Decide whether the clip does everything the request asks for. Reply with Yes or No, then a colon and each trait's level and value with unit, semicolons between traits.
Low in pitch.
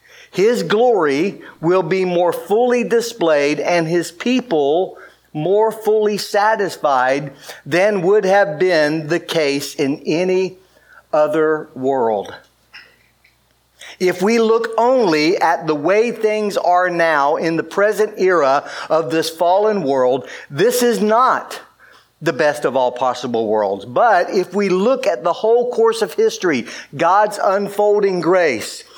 No: medium, 185 Hz